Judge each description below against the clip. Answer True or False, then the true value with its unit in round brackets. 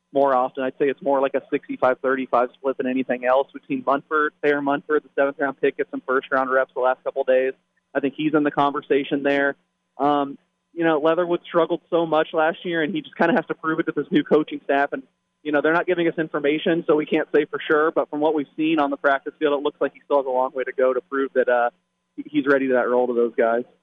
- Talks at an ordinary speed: False (270 wpm)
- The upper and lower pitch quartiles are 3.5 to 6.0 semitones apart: False (3.1 semitones)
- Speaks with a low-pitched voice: False (145 Hz)